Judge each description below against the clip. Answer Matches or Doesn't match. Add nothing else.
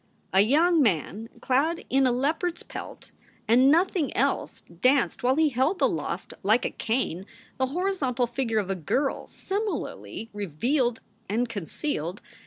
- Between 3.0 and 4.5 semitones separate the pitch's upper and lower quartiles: Doesn't match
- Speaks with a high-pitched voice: Matches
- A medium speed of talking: Matches